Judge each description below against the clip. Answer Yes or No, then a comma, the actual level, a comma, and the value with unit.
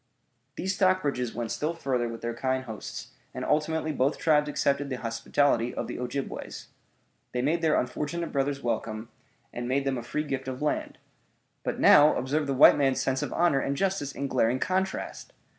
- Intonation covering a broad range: No, average, 3.4 semitones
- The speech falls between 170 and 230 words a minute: Yes, average, 180 wpm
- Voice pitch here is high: No, medium, 140 Hz